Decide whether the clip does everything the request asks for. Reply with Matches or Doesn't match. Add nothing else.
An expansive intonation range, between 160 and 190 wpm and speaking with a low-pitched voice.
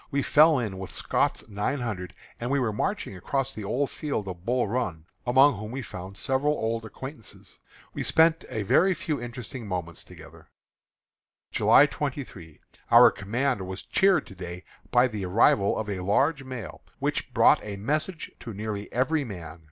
Matches